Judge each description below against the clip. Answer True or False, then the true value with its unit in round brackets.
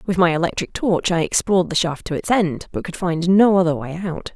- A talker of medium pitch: True (175 Hz)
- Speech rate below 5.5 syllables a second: False (5.6 syllables/s)